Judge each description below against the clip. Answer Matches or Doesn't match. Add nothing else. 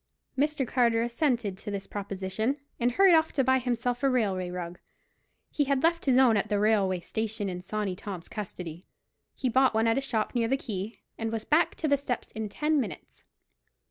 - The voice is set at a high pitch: Matches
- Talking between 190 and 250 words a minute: Matches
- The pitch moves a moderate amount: Matches